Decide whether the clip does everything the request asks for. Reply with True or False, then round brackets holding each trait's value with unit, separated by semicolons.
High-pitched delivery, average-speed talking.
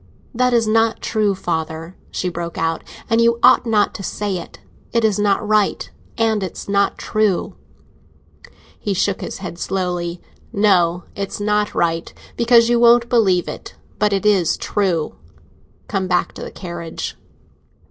True (200 Hz; 155 wpm)